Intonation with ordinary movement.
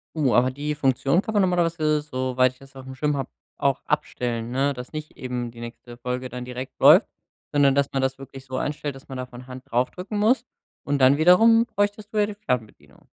Yes: average, 3.5 semitones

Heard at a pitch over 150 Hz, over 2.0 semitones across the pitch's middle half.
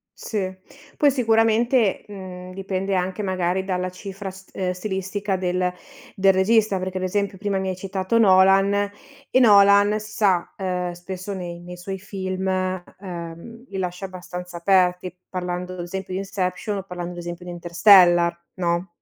No: high, 190 Hz; narrow, 1.7 semitones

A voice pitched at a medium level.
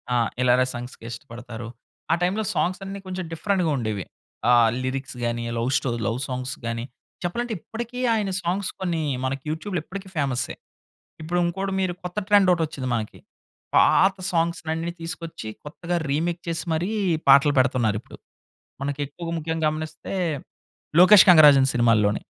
Yes: medium, 160 Hz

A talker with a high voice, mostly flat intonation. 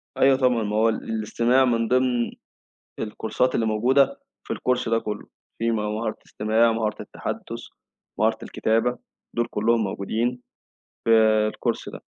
No: low, 115 Hz; narrow, 2.1 semitones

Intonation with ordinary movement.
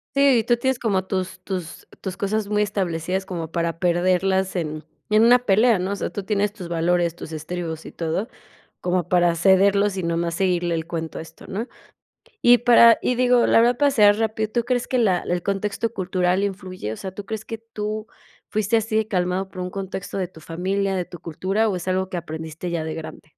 Yes: average, 3.5 semitones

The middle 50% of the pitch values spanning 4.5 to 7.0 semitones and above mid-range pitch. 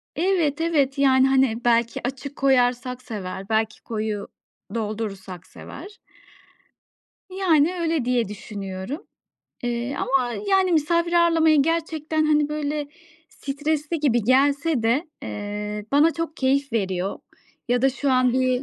Yes: average, 5.1 semitones; very high, 270 Hz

